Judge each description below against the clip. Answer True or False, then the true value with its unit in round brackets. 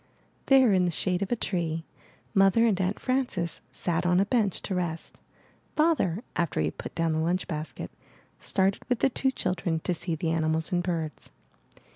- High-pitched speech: False (180 Hz)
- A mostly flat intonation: False (3.5 semitones)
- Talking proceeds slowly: False (185 wpm)